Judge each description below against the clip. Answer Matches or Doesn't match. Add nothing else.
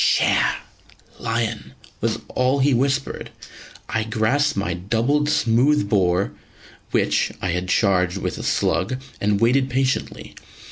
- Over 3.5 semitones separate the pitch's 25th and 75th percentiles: Matches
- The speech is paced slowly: Matches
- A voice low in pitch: Matches